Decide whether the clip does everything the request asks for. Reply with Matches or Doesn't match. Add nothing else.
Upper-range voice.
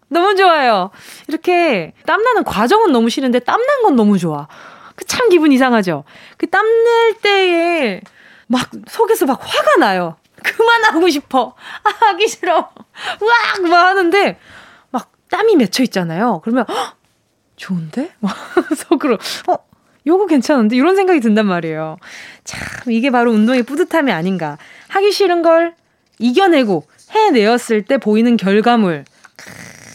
Matches